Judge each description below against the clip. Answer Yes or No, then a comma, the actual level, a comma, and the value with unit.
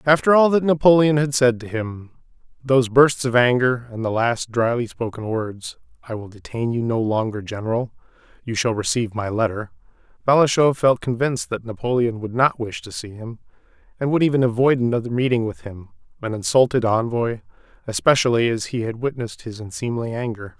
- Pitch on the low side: Yes, low, 120 Hz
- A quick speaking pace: No, average, 165 wpm